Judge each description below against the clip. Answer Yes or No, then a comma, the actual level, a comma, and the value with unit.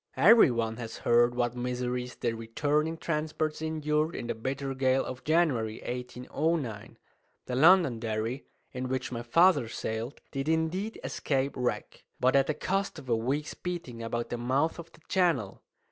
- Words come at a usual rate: Yes, average, 160 wpm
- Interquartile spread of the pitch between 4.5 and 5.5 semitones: Yes, average, 4.8 semitones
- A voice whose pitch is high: No, low, 130 Hz